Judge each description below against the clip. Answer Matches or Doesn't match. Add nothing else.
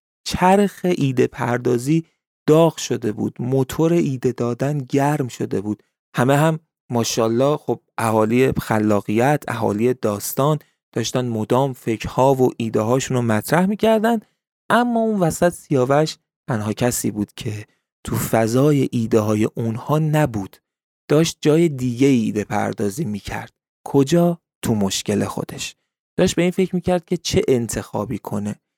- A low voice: Matches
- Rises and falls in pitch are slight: Doesn't match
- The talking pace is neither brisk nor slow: Matches